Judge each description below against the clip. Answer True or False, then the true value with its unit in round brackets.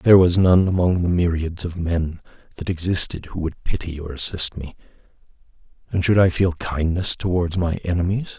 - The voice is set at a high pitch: False (85 Hz)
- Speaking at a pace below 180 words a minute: True (170 wpm)